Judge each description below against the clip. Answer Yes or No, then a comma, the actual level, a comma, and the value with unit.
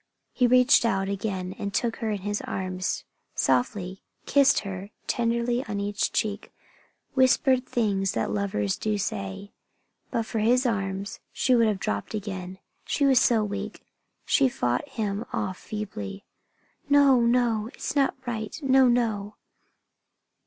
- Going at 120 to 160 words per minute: Yes, average, 145 wpm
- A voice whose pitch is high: Yes, high, 210 Hz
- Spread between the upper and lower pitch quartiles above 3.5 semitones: Yes, average, 3.9 semitones